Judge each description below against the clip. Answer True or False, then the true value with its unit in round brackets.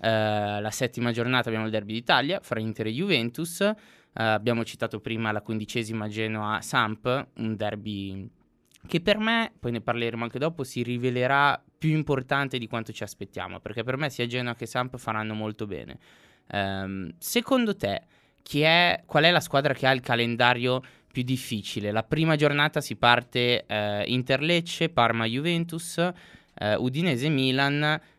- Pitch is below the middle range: True (120 Hz)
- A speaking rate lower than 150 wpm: False (155 wpm)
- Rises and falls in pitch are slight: False (4.9 semitones)